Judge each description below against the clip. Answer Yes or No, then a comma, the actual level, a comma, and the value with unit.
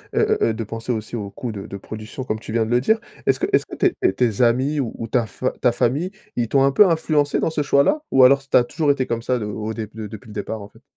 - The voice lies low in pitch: Yes, low, 120 Hz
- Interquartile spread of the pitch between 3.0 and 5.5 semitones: Yes, average, 4.0 semitones